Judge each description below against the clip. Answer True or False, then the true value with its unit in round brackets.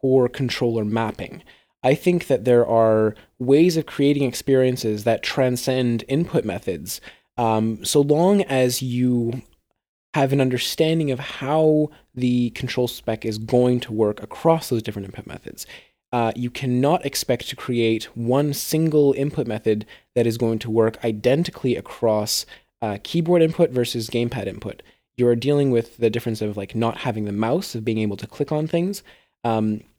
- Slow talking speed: False (160 wpm)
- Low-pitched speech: True (125 Hz)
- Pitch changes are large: False (3.8 semitones)